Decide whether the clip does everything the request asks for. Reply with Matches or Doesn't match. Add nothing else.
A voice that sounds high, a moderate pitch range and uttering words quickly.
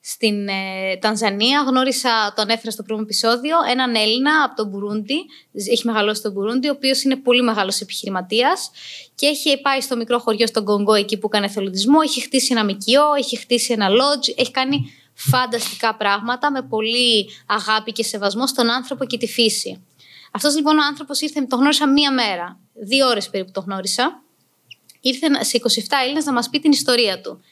Matches